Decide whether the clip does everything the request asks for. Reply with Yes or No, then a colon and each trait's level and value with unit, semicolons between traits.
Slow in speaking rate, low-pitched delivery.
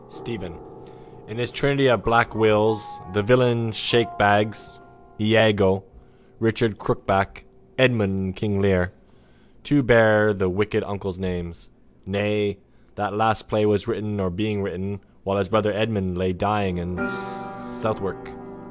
Yes: slow, 130 wpm; low, 105 Hz